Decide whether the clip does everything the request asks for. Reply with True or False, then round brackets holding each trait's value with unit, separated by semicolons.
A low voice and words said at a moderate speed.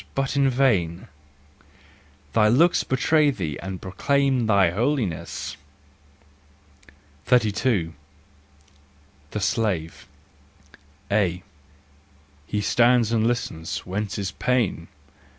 False (110 Hz; 85 wpm)